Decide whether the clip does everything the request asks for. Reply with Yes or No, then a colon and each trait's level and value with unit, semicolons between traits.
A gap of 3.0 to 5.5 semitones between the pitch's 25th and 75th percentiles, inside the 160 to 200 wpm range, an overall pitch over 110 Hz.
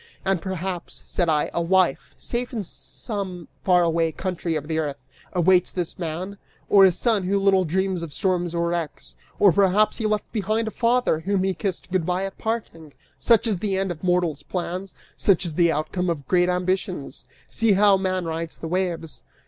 No: narrow, 2.6 semitones; average, 190 wpm; medium, 185 Hz